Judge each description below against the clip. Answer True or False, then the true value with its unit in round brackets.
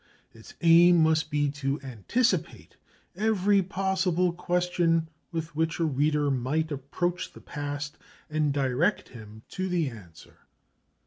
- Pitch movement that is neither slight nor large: True (4.0 semitones)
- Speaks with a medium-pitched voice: True (160 Hz)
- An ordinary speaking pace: False (125 wpm)